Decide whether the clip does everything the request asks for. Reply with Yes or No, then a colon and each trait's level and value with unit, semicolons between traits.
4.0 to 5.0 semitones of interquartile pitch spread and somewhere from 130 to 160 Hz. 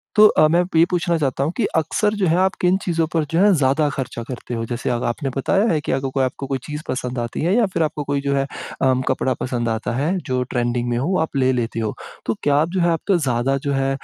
Yes: average, 4.7 semitones; medium, 140 Hz